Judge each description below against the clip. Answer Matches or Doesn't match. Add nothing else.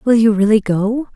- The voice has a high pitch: Matches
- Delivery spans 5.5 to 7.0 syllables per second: Doesn't match